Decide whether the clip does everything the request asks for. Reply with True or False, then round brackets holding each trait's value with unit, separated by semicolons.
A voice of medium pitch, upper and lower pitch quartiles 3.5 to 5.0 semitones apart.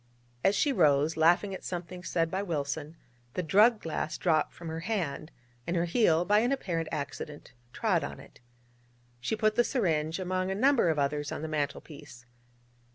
True (170 Hz; 4.2 semitones)